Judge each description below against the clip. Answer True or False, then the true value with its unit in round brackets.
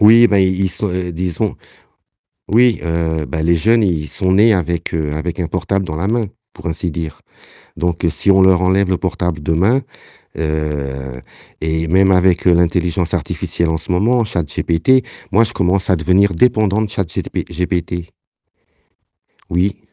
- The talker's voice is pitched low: True (90 Hz)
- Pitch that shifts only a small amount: False (3.2 semitones)